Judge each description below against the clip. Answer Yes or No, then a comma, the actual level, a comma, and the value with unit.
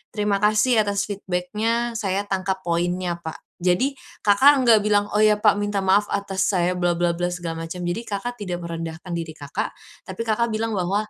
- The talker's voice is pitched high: Yes, high, 195 Hz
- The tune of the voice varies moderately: Yes, average, 3.2 semitones